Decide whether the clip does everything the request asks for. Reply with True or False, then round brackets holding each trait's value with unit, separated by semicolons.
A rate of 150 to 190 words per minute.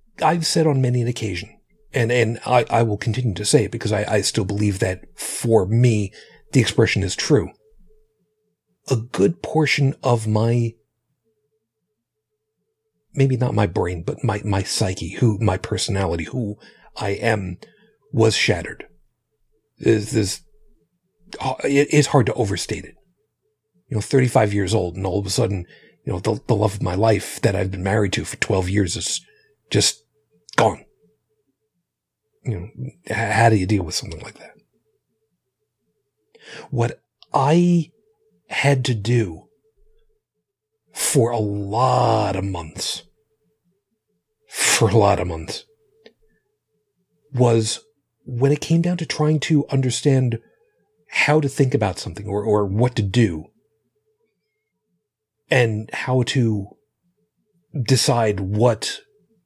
False (135 wpm)